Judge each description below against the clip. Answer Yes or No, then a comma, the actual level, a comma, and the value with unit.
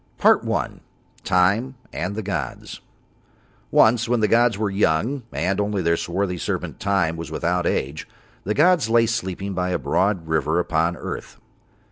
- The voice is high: No, very low, 95 Hz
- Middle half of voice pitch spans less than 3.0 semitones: No, average, 4.2 semitones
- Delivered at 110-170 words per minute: Yes, average, 155 wpm